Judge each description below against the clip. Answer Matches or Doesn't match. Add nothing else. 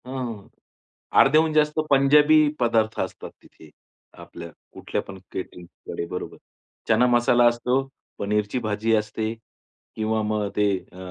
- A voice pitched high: Doesn't match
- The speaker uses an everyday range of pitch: Matches